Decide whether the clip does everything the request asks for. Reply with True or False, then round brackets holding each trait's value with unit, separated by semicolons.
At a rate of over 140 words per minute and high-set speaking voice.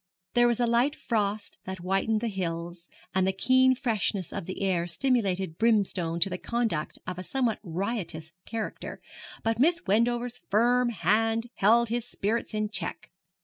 True (155 wpm; 215 Hz)